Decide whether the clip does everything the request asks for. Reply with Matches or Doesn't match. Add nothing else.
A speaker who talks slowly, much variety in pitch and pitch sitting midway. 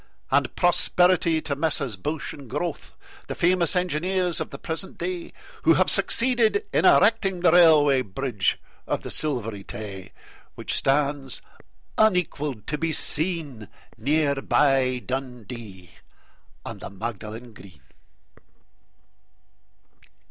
Matches